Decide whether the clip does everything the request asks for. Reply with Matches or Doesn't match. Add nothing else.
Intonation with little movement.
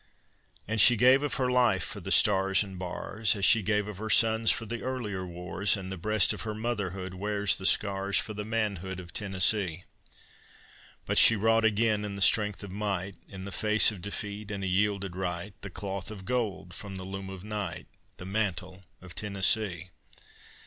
Matches